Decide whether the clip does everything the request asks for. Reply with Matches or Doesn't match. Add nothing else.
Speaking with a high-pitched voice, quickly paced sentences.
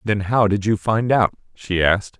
Doesn't match